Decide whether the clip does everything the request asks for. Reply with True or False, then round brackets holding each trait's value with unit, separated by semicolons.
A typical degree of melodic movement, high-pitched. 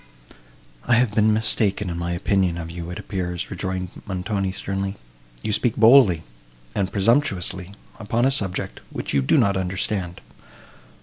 False (3.2 semitones; 95 Hz)